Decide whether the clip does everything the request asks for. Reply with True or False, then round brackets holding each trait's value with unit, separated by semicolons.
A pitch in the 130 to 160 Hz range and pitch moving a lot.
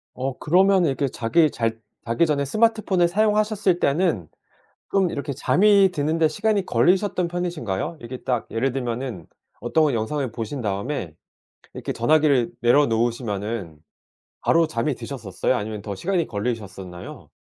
True (135 Hz; 7.1 semitones)